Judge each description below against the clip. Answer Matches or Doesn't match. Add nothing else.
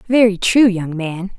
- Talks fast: Doesn't match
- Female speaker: Matches